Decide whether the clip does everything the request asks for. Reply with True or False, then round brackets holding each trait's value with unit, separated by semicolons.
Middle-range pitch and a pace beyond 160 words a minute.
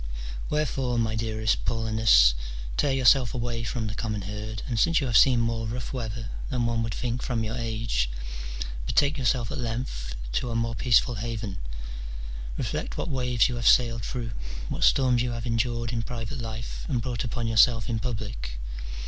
False (115 Hz; 175 wpm)